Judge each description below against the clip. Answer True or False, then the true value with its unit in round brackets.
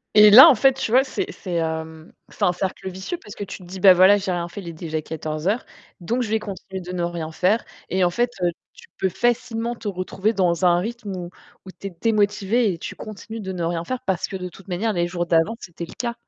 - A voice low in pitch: False (190 Hz)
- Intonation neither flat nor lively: True (4.1 semitones)